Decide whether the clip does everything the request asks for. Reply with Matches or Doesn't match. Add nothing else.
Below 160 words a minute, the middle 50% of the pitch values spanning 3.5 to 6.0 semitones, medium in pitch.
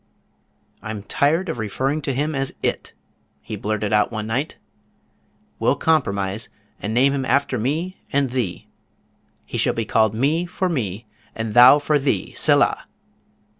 Doesn't match